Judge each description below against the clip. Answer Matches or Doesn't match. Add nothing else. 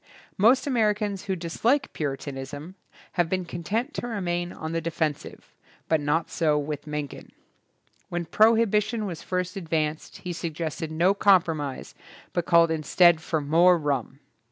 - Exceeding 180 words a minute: Doesn't match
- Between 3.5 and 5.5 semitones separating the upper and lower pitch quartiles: Matches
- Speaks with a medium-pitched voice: Matches